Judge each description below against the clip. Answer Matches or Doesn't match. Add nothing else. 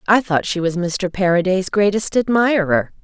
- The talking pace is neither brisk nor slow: Matches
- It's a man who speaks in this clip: Doesn't match